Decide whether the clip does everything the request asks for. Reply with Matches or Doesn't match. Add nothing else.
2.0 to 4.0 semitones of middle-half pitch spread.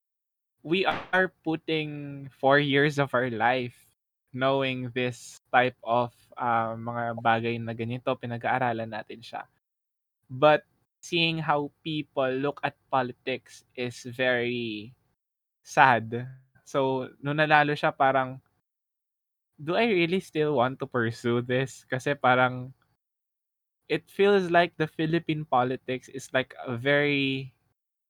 Matches